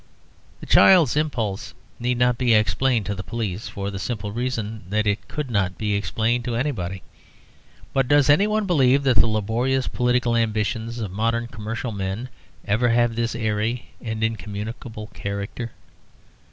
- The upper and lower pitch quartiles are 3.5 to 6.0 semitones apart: No, average, 2.9 semitones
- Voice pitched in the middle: No, low, 115 Hz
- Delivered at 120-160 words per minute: Yes, average, 155 wpm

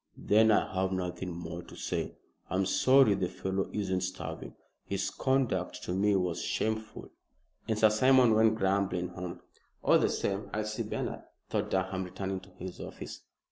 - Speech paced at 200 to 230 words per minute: No, average, 165 wpm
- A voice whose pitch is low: Yes, very low, 95 Hz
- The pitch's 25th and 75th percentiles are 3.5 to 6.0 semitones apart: No, average, 2.8 semitones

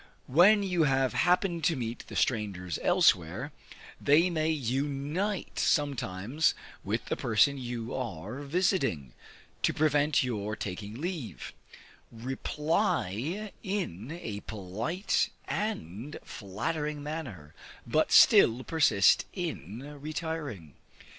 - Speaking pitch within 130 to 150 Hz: Yes, low, 135 Hz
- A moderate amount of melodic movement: No, wide, 7.1 semitones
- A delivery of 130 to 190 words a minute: No, slow, 100 wpm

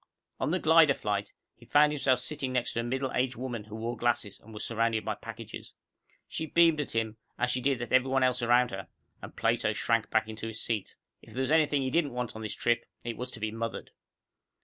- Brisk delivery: Yes, fast, 235 wpm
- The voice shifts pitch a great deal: No, average, 2.8 semitones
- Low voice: Yes, low, 120 Hz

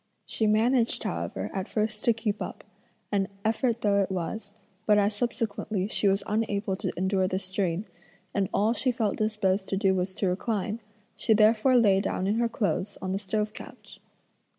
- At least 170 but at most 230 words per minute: Yes, average, 180 wpm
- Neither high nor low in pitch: No, high, 210 Hz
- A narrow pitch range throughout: Yes, narrow, 2.3 semitones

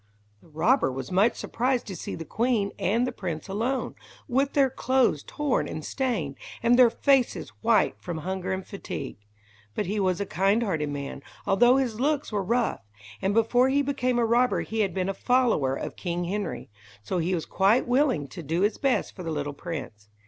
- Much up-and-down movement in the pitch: Yes, wide, 6.3 semitones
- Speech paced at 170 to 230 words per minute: Yes, average, 190 wpm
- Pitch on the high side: Yes, high, 205 Hz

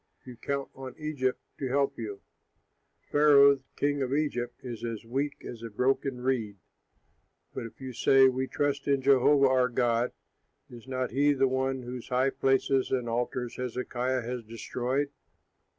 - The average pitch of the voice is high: No, low, 130 Hz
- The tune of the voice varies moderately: No, narrow, 2.0 semitones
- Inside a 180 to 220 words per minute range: No, average, 155 wpm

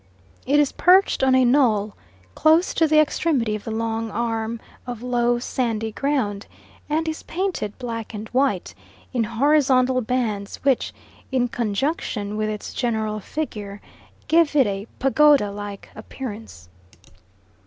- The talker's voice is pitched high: Yes, high, 240 Hz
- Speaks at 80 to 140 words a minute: Yes, slow, 135 wpm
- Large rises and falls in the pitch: No, average, 4.6 semitones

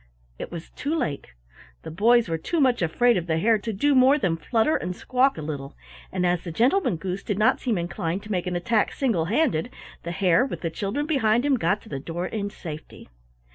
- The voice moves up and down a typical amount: No, wide, 6.3 semitones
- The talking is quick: Yes, fast, 220 wpm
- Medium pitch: No, high, 200 Hz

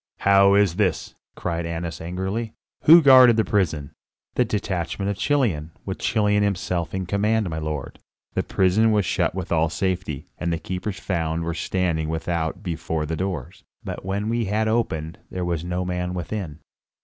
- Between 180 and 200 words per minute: No, average, 170 wpm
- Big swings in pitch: No, average, 3.7 semitones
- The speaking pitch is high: No, very low, 90 Hz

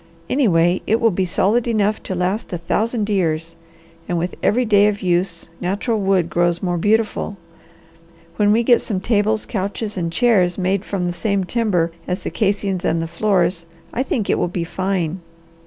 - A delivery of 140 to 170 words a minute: No, average, 180 wpm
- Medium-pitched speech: No, high, 195 Hz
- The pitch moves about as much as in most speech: Yes, average, 3.4 semitones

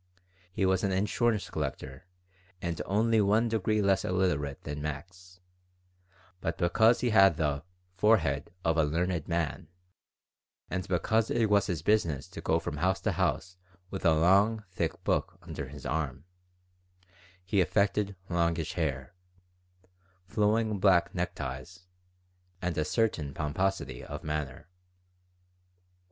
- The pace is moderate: No, slow, 130 wpm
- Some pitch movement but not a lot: Yes, average, 4.2 semitones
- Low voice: Yes, very low, 90 Hz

